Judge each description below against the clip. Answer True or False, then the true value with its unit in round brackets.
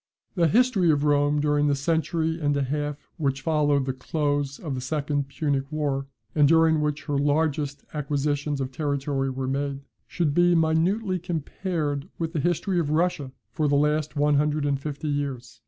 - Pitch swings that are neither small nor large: False (2.1 semitones)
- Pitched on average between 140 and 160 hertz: True (145 Hz)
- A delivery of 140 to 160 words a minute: False (175 wpm)